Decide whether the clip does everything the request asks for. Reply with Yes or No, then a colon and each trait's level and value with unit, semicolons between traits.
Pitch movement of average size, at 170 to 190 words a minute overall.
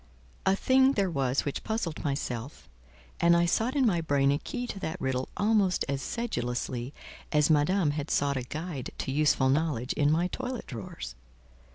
No: wide, 6.1 semitones; average, 175 wpm